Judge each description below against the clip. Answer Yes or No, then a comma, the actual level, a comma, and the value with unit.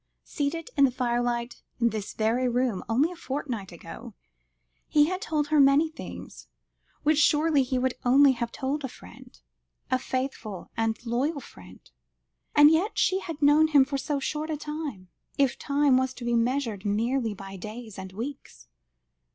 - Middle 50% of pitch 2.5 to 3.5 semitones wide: No, average, 4.2 semitones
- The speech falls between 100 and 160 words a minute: No, average, 170 wpm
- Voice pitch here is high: Yes, very high, 260 Hz